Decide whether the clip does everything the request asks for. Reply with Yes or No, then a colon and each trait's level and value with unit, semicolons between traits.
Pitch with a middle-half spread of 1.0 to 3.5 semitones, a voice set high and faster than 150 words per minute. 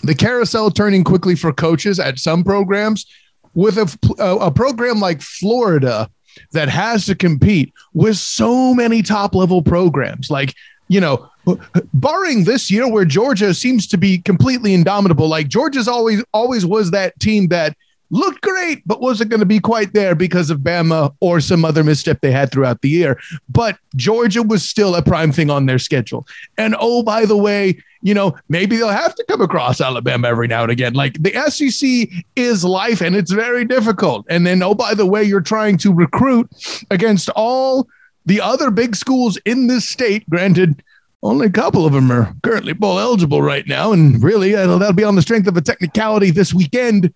No: average, 5.1 semitones; high, 195 Hz; average, 185 wpm